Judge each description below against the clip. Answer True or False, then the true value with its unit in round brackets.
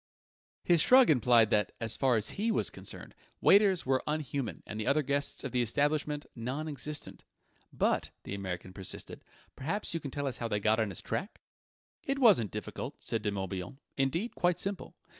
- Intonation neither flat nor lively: False (6.0 semitones)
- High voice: False (135 Hz)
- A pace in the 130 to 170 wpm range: False (180 wpm)